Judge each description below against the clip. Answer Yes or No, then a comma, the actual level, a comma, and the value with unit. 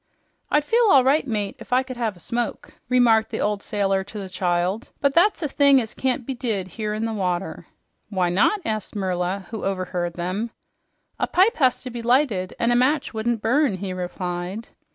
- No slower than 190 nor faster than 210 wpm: Yes, average, 200 wpm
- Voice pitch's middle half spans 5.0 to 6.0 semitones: Yes, average, 5.3 semitones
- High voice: Yes, high, 220 Hz